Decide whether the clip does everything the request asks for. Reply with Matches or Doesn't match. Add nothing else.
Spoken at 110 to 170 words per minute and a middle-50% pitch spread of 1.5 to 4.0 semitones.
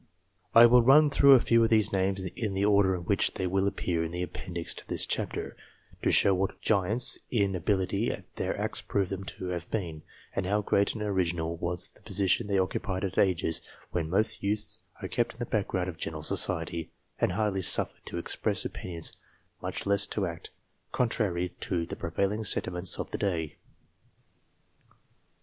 Doesn't match